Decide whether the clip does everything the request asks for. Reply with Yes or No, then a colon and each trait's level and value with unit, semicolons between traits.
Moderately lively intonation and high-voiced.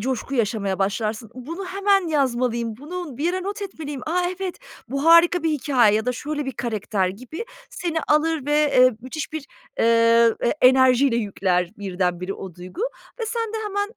No: wide, 6.7 semitones; very high, 260 Hz